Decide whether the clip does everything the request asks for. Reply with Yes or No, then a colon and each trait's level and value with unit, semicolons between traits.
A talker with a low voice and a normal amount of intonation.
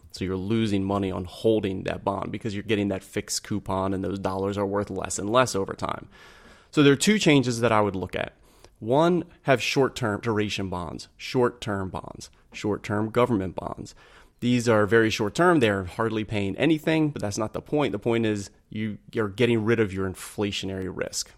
Yes: low, 105 Hz; average, 3.7 semitones